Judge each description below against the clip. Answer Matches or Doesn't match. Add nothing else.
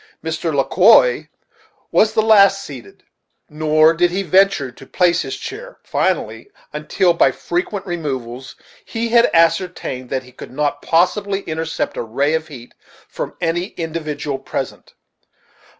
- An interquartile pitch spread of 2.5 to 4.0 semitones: Doesn't match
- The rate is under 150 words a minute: Matches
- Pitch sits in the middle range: Matches